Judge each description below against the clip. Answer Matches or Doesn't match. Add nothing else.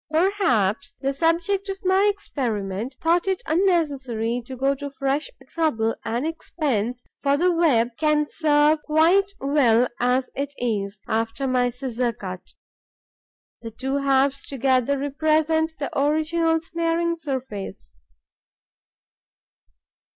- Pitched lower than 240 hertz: Doesn't match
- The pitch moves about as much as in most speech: Matches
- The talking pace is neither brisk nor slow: Doesn't match